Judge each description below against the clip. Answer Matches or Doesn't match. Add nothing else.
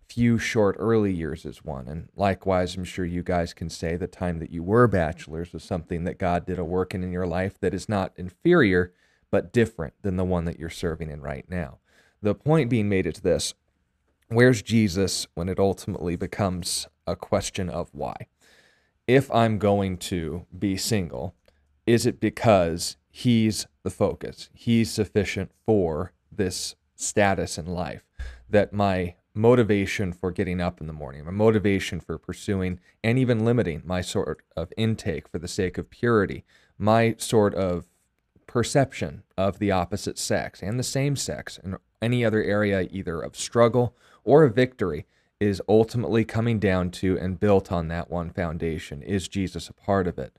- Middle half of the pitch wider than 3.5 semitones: Matches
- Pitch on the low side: Matches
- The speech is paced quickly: Doesn't match